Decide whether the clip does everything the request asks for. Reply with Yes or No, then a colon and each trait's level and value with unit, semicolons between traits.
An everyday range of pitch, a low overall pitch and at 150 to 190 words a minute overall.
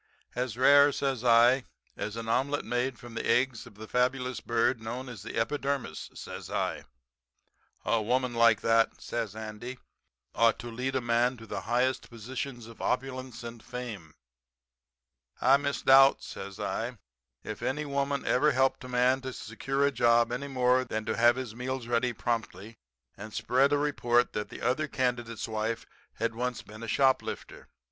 No: narrow, 2.3 semitones; low, 125 Hz; average, 170 wpm